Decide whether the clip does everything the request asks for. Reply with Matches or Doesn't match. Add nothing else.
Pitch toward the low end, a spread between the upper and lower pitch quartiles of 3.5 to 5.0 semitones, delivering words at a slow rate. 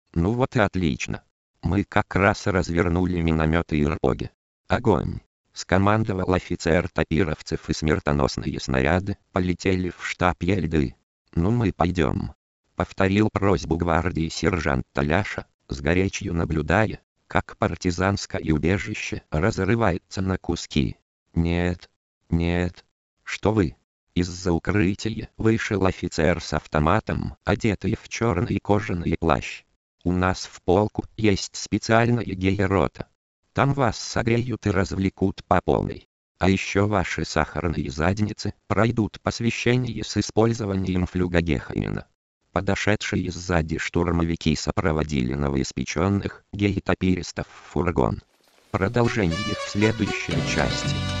Matches